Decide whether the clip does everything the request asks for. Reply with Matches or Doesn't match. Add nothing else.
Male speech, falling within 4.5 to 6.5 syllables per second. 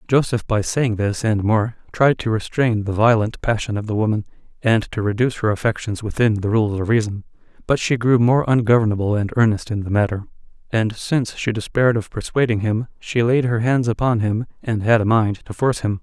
Matches